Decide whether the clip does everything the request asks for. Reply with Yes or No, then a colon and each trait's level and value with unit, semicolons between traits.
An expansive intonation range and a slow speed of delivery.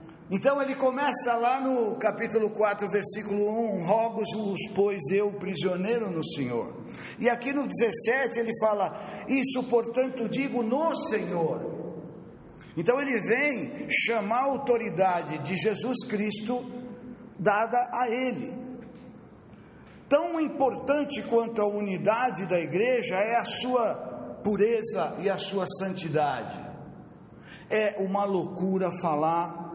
No: average, 3.8 semitones; slow, 115 wpm